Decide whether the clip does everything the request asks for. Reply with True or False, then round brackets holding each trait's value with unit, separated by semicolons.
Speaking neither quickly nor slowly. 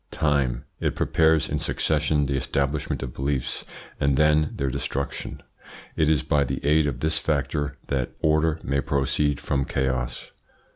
True (150 wpm)